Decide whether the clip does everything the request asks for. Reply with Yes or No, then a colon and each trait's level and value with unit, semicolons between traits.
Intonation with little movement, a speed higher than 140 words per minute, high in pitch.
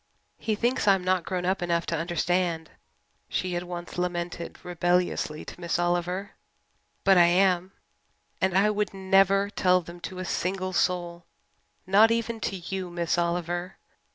No: narrow, 1.8 semitones; average, 155 wpm; medium, 180 Hz